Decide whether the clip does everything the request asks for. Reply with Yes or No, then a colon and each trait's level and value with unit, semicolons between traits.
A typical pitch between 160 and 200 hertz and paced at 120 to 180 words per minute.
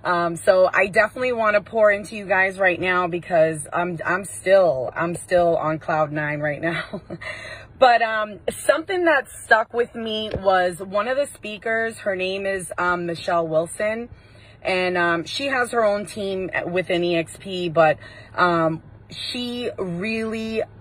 Yes: high, 190 Hz; average, 155 wpm